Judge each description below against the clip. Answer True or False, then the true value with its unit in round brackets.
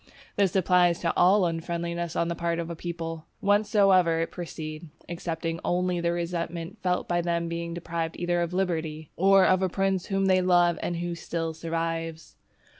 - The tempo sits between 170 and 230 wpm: True (180 wpm)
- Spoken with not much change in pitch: True (1.5 semitones)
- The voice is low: False (170 Hz)